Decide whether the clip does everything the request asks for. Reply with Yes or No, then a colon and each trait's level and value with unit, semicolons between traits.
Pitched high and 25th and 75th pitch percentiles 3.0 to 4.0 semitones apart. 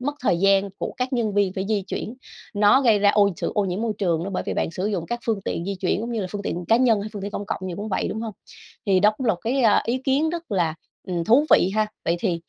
Yes: high, 205 Hz; average, 3.4 semitones